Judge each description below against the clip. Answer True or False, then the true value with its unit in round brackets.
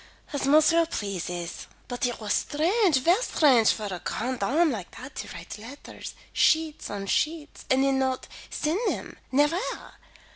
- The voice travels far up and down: True (6.0 semitones)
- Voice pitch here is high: True (270 Hz)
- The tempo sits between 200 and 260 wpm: False (155 wpm)